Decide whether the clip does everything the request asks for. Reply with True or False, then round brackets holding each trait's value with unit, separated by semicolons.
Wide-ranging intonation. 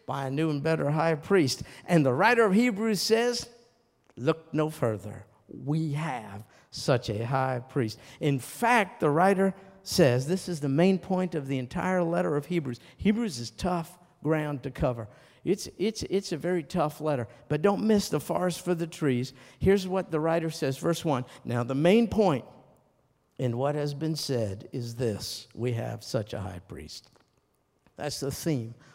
True (5.7 semitones)